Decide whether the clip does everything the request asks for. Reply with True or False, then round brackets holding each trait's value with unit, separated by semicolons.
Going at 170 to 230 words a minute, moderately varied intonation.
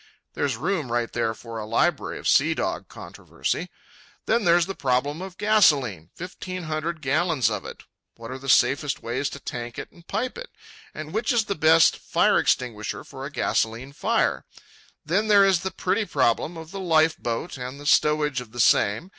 False (185 wpm; 6.7 semitones)